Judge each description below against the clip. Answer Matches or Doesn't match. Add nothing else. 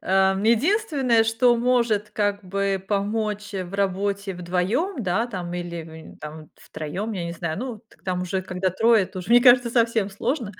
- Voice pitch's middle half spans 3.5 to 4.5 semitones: Matches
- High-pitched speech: Matches